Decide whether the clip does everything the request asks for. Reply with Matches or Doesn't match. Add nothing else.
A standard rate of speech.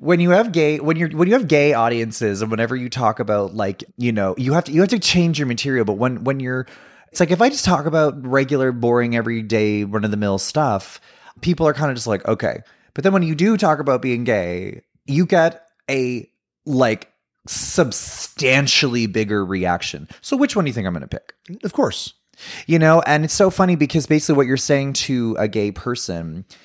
Doesn't match